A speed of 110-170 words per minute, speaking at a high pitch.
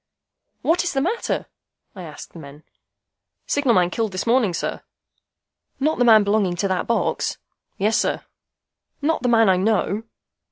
Yes: average, 160 wpm; high, 220 Hz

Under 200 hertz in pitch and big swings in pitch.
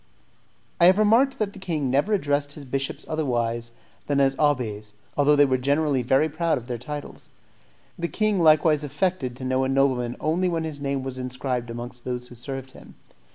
No: medium, 140 Hz; average, 3.7 semitones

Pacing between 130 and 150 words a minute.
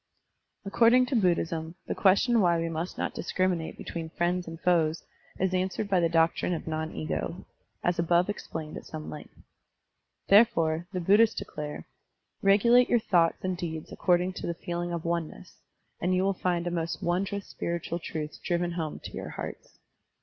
No: average, 170 wpm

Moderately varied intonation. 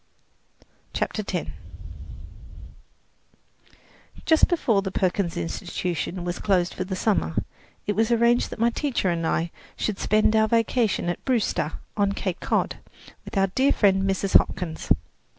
Yes: average, 4.0 semitones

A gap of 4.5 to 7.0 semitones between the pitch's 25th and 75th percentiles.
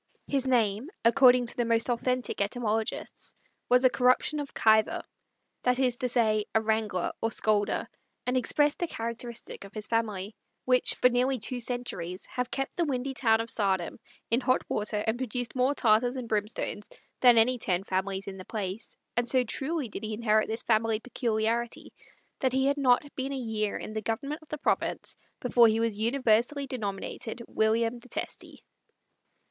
No: average, 2.7 semitones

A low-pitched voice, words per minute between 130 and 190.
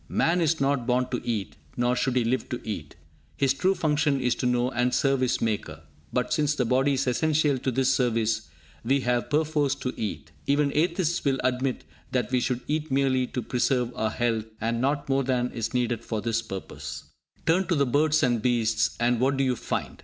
No: low, 130 Hz; fast, 205 wpm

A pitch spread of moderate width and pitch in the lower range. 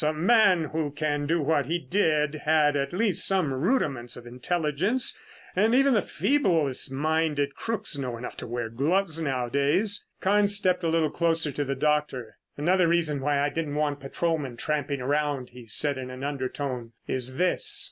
No: average, 3.8 semitones; medium, 150 Hz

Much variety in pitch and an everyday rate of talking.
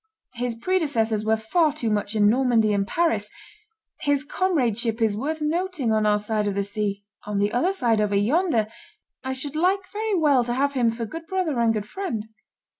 Yes: wide, 6.6 semitones; average, 190 wpm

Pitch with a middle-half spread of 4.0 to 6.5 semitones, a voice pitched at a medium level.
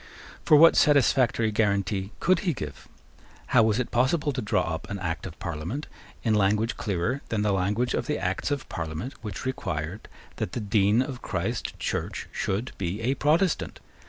No: wide, 5.4 semitones; low, 110 Hz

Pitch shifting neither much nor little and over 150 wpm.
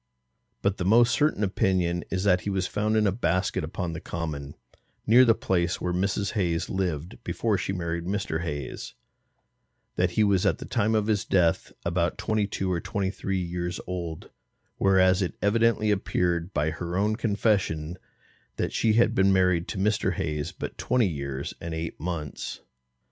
Yes: average, 3.2 semitones; average, 175 wpm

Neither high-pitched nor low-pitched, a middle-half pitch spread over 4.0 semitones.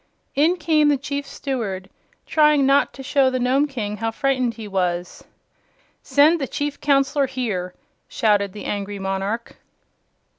No: very high, 255 Hz; wide, 5.6 semitones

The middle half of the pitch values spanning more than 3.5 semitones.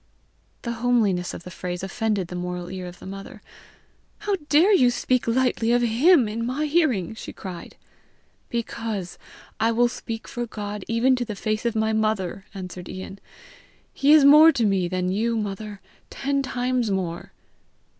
Yes: average, 4.4 semitones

